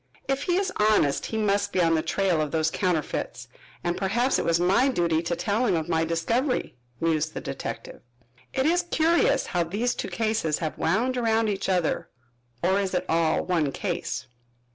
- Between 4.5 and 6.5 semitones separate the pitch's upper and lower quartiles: Yes, wide, 5.6 semitones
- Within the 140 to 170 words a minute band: No, average, 185 wpm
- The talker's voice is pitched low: No, high, 190 Hz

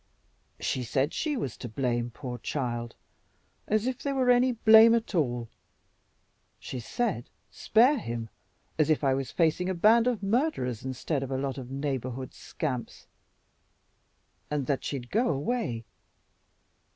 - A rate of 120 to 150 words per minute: Yes, average, 145 wpm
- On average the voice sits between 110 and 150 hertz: Yes, medium, 140 Hz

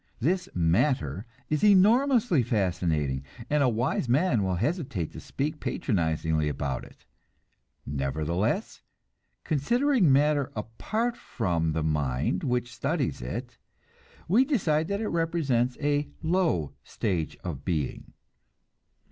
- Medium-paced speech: No, slow, 115 wpm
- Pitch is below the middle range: Yes, low, 125 Hz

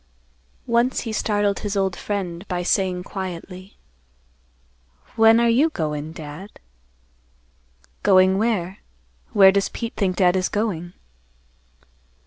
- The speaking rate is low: Yes, slow, 115 wpm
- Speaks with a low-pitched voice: No, high, 190 Hz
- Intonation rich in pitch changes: No, average, 2.9 semitones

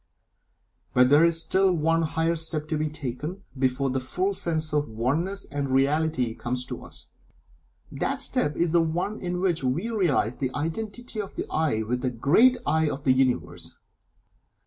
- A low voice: No, medium, 155 Hz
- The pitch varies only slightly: No, average, 4.7 semitones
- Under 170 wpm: No, average, 175 wpm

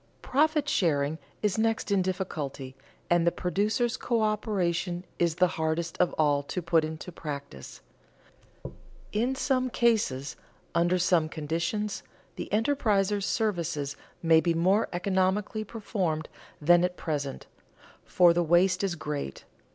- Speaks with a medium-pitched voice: Yes, medium, 180 Hz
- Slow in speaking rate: Yes, slow, 120 wpm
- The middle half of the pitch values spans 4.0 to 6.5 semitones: Yes, average, 4.7 semitones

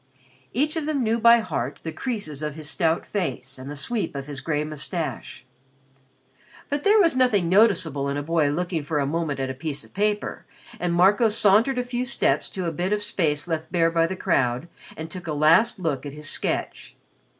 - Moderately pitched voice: Yes, medium, 170 Hz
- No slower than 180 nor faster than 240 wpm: Yes, fast, 205 wpm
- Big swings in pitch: Yes, wide, 6.1 semitones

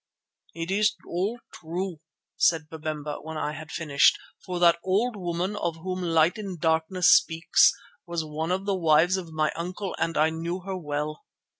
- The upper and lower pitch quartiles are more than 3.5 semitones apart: No, average, 2.7 semitones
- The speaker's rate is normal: Yes, average, 175 wpm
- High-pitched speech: No, medium, 170 Hz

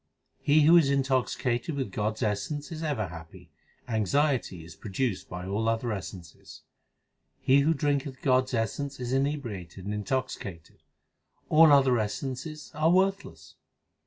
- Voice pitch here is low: Yes, low, 130 Hz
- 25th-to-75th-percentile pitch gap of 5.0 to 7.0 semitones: Yes, wide, 5.6 semitones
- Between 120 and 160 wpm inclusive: Yes, average, 145 wpm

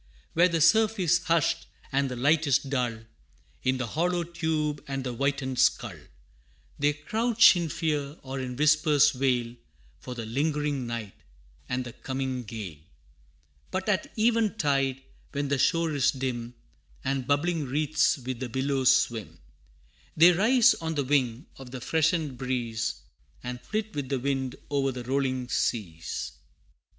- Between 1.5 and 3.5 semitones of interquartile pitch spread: No, average, 4.0 semitones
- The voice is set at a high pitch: No, medium, 140 Hz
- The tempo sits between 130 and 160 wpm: Yes, average, 150 wpm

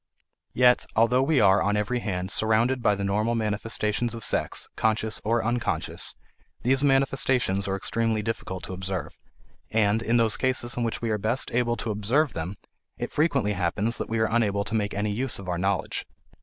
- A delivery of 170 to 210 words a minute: Yes, average, 185 wpm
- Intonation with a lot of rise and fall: No, average, 2.8 semitones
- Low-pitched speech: Yes, low, 110 Hz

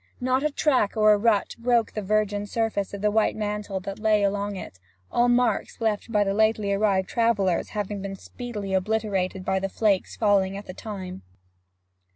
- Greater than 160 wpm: Yes, average, 180 wpm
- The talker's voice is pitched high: Yes, high, 205 Hz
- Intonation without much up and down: Yes, narrow, 2.1 semitones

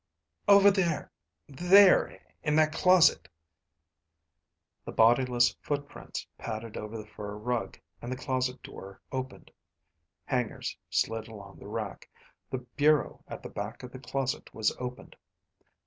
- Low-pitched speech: Yes, low, 125 Hz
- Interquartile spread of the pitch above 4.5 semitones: Yes, average, 4.9 semitones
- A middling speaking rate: No, slow, 130 wpm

